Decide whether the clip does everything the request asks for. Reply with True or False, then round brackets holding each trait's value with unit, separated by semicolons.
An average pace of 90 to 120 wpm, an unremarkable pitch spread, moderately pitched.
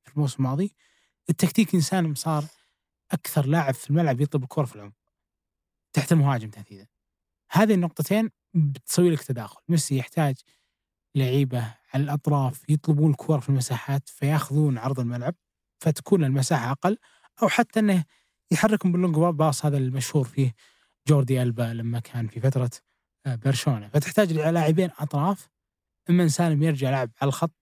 False (135 wpm; 4.1 semitones; 150 Hz)